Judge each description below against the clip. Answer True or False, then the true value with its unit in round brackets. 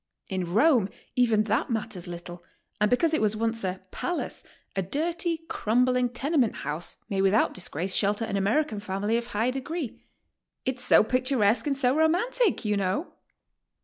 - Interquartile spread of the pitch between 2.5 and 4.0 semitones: False (5.5 semitones)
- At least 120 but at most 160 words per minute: True (155 wpm)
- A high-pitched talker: True (225 Hz)